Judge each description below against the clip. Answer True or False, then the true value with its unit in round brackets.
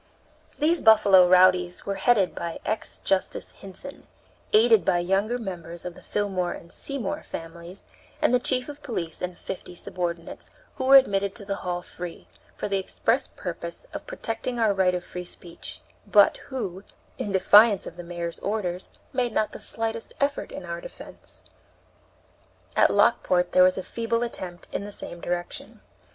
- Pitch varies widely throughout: False (4.4 semitones)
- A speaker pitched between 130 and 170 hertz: False (195 Hz)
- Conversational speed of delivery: True (165 wpm)